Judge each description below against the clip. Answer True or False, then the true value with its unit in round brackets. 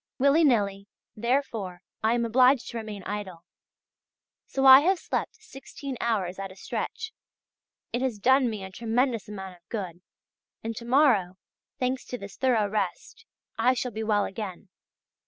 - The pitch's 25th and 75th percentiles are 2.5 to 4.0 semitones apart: False (4.7 semitones)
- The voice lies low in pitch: False (225 Hz)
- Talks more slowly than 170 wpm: True (155 wpm)